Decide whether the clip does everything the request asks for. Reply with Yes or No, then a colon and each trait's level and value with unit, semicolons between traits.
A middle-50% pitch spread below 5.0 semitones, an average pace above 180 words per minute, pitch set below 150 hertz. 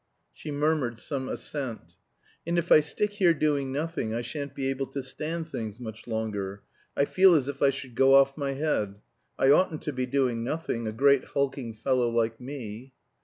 Yes: average, 4.0 semitones; average, 190 wpm; low, 135 Hz